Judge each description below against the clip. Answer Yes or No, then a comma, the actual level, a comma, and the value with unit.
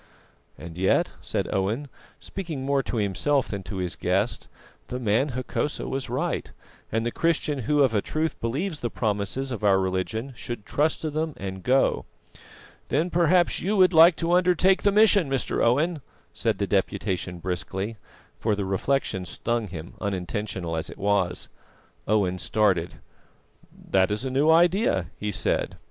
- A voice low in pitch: Yes, low, 120 Hz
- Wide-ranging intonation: Yes, wide, 8.0 semitones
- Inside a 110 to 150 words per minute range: No, average, 160 wpm